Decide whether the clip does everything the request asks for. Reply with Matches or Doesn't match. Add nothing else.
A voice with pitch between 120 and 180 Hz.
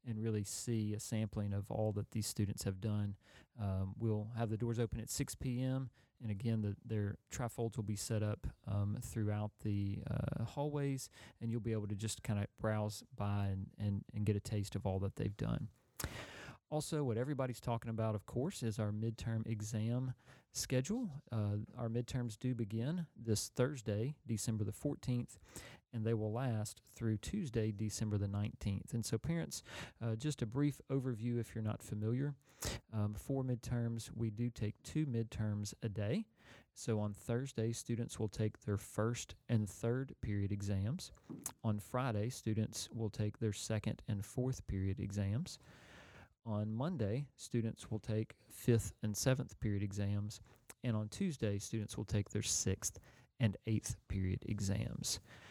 Doesn't match